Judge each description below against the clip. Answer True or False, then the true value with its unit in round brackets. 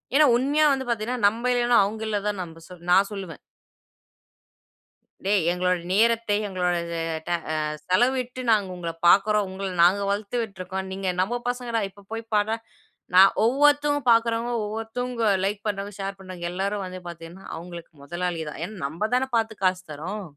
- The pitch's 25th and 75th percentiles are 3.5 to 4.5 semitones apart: True (4.0 semitones)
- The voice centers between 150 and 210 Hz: True (205 Hz)